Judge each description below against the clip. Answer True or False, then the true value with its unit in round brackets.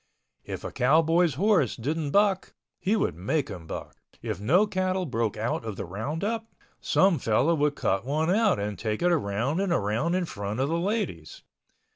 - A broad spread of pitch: True (8.9 semitones)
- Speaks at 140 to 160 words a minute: False (180 wpm)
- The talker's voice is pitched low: False (150 Hz)